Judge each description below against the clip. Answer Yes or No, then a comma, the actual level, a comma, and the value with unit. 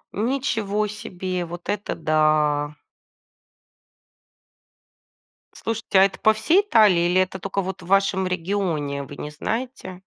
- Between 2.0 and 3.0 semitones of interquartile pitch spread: No, average, 3.8 semitones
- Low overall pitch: No, high, 190 Hz